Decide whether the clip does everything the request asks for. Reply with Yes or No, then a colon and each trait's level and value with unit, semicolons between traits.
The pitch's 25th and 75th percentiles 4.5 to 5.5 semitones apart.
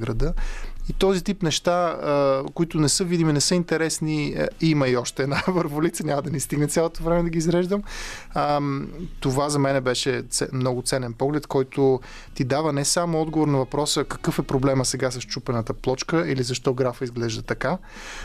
No: average, 3.8 semitones